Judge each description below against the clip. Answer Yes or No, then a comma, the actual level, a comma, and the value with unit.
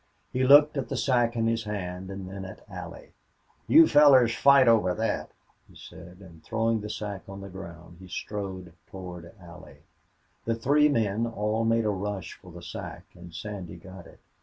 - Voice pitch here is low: Yes, low, 105 Hz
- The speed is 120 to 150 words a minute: No, average, 185 wpm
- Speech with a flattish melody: No, average, 3.8 semitones